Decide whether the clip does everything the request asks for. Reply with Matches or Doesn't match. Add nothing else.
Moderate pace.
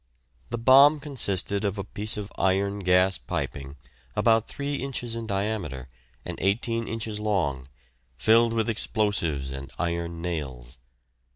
Doesn't match